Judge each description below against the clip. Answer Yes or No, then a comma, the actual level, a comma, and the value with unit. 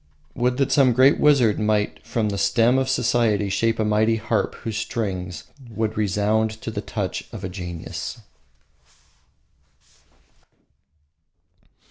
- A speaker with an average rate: No, slow, 120 wpm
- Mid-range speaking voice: No, low, 110 Hz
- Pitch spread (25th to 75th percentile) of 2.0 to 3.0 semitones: Yes, narrow, 2.5 semitones